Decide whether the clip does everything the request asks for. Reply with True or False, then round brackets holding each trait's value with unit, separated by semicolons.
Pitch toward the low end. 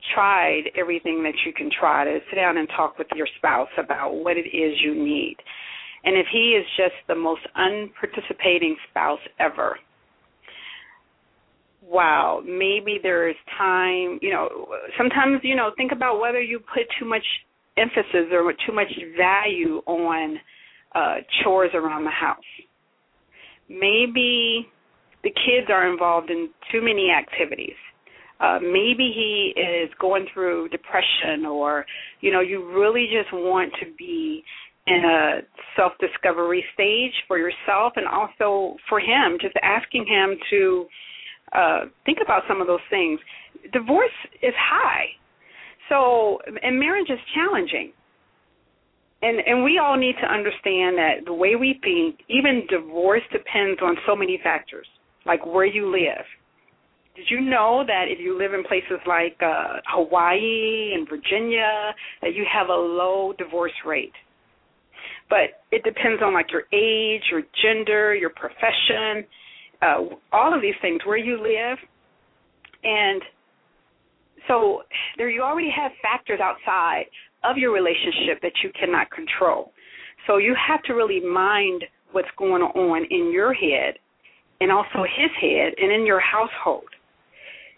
False (210 Hz)